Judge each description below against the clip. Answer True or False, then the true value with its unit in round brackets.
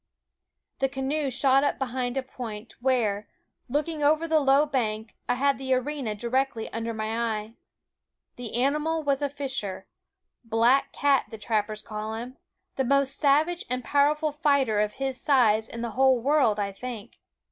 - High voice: True (260 Hz)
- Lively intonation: False (4.0 semitones)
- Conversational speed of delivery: True (160 wpm)